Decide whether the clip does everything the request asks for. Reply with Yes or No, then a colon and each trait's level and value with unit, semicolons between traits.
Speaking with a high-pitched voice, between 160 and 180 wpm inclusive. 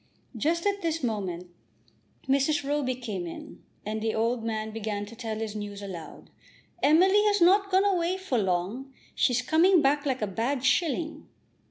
Yes: very high, 255 Hz; average, 165 wpm